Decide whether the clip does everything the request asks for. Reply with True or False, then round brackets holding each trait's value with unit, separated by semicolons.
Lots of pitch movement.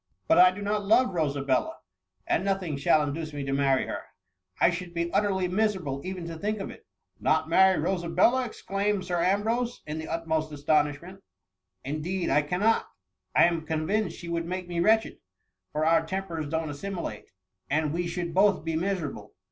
False (3.7 semitones)